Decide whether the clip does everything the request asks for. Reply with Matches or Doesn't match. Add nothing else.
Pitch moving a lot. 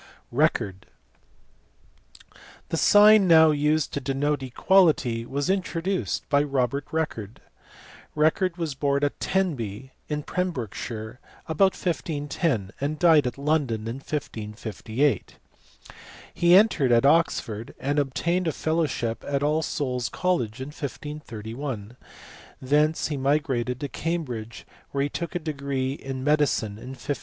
Doesn't match